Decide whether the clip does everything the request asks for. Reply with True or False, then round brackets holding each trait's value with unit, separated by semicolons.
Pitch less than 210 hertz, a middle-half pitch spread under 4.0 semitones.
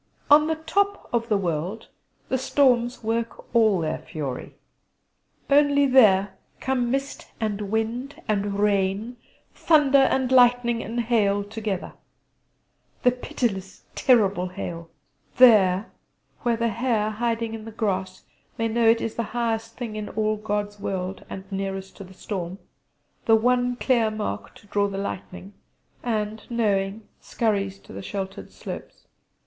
False (220 Hz; 3.5 semitones)